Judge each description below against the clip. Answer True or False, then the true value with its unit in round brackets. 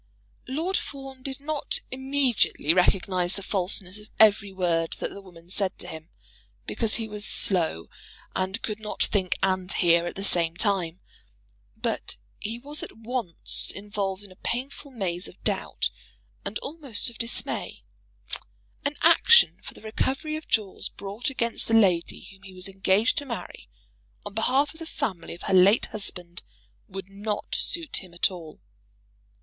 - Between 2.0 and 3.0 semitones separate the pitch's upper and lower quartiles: False (5.1 semitones)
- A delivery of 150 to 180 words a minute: True (160 wpm)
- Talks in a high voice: True (205 Hz)